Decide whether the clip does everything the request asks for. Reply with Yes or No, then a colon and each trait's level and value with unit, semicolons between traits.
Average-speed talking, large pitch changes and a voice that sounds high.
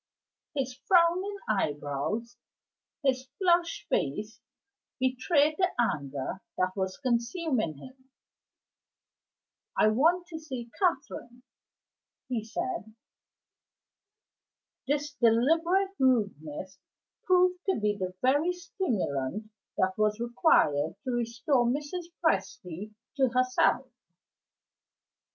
No: slow, 90 wpm; wide, 7.5 semitones; very high, 250 Hz